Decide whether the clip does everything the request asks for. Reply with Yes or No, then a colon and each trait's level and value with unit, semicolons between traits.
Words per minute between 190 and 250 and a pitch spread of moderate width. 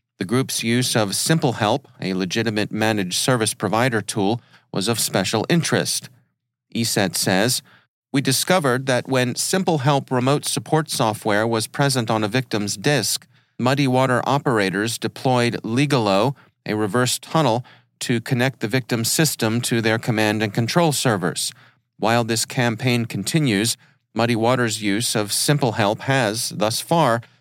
No: average, 140 wpm; average, 3.5 semitones